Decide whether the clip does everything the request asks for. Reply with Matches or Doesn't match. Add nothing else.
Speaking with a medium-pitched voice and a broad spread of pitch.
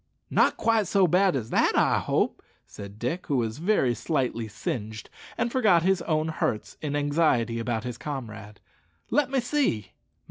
Matches